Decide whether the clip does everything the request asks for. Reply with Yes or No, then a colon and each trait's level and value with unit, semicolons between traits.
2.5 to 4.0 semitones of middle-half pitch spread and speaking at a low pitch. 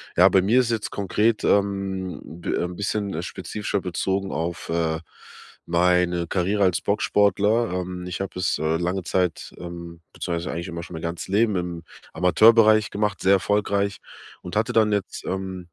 Yes: average, 2.8 semitones; very low, 95 Hz